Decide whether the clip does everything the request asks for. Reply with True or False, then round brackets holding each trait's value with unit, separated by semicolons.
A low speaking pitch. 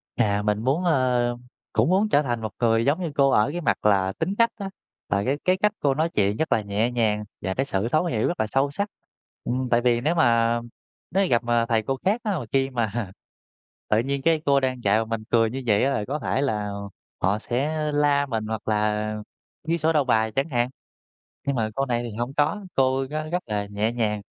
True (125 Hz)